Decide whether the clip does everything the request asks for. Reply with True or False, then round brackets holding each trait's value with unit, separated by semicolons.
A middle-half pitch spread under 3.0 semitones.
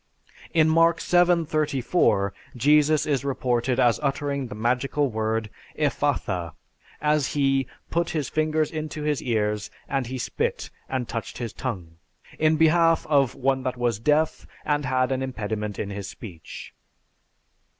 False (4.7 semitones)